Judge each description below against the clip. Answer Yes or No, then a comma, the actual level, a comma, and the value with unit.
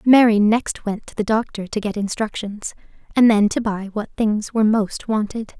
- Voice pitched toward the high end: Yes, high, 215 Hz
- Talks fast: No, average, 195 wpm